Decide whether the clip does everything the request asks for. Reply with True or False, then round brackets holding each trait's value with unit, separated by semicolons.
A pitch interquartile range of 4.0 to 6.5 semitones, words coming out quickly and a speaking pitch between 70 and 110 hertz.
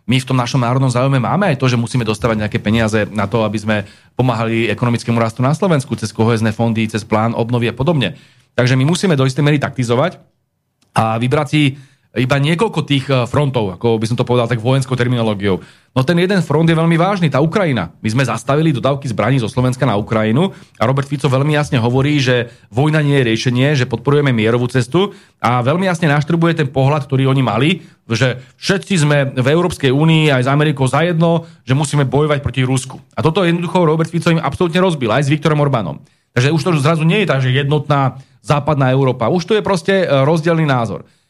False (4.5 semitones; 200 wpm; 135 Hz)